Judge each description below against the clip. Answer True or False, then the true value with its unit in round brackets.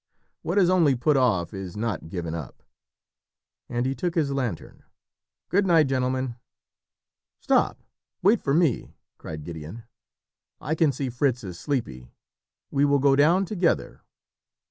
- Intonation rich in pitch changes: True (7.1 semitones)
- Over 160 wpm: False (140 wpm)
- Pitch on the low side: True (130 Hz)